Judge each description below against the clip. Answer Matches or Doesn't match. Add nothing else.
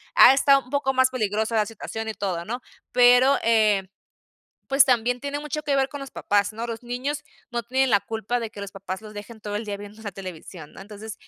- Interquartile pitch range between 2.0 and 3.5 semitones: Doesn't match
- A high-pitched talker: Matches